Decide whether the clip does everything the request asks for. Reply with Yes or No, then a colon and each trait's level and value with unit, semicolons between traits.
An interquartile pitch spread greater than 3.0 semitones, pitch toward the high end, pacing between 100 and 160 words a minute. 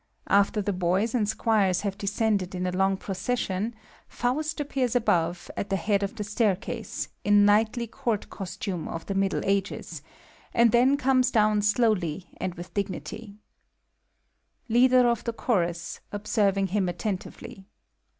Yes: average, 3.4 semitones; high, 205 Hz; average, 140 wpm